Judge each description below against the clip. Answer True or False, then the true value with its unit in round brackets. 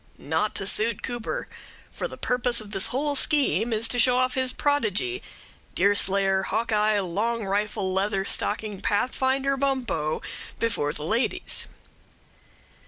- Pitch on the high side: True (220 Hz)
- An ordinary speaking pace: False (130 wpm)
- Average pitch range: True (4.4 semitones)